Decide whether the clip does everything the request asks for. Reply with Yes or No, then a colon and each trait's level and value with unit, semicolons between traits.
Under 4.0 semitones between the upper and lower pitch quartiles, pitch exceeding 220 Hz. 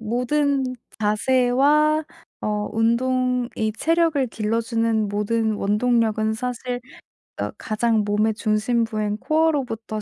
Yes: average, 2.9 semitones; high, 230 Hz